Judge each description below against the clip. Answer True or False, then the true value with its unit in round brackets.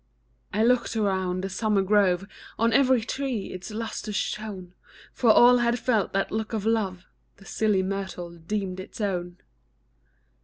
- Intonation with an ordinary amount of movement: True (3.1 semitones)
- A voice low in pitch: False (205 Hz)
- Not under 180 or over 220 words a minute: False (150 wpm)